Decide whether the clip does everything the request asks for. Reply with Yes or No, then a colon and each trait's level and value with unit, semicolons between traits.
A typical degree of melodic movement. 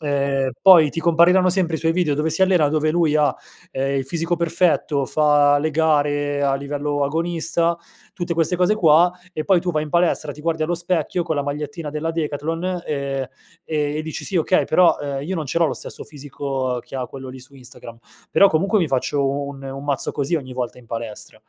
Yes: average, 3.2 semitones